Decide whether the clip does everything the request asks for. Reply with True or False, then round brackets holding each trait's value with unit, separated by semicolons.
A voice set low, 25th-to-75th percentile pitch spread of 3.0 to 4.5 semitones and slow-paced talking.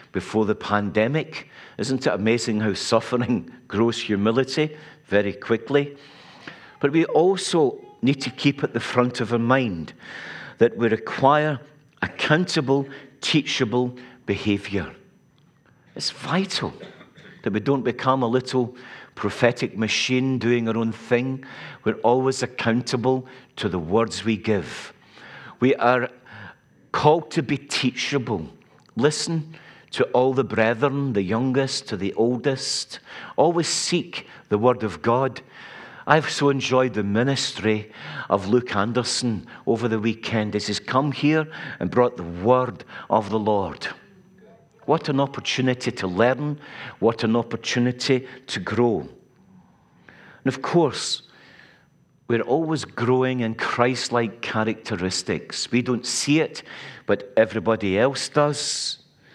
True (125 Hz; 3.7 semitones; 125 wpm)